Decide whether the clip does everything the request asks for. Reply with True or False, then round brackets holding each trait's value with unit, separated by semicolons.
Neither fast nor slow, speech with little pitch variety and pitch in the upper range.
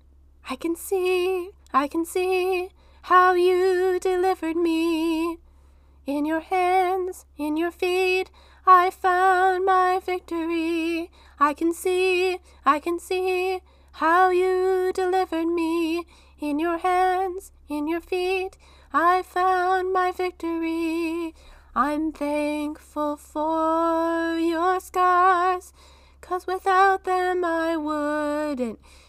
False (105 wpm; 2.2 semitones; 355 Hz)